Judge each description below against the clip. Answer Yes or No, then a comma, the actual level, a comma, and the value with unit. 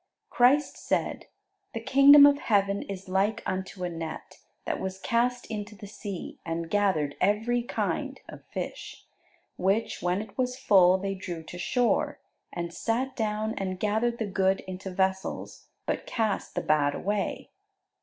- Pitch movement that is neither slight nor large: Yes, average, 3.4 semitones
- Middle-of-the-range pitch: No, high, 200 Hz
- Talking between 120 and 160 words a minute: Yes, average, 155 wpm